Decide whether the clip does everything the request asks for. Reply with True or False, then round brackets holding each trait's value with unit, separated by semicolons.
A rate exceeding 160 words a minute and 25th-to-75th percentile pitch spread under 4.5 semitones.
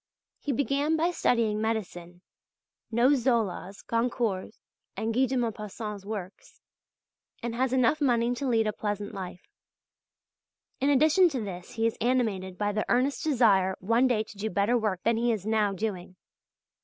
False (155 wpm; 3.5 semitones)